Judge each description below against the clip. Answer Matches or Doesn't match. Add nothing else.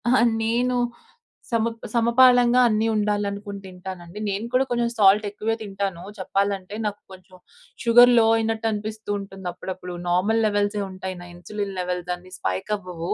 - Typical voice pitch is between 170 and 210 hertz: Matches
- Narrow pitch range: Doesn't match